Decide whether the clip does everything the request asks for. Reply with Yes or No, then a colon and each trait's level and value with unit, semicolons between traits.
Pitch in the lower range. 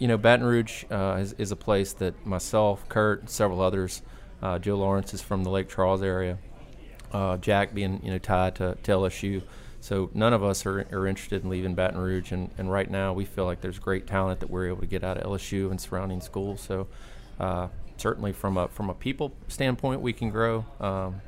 Yes: very low, 95 Hz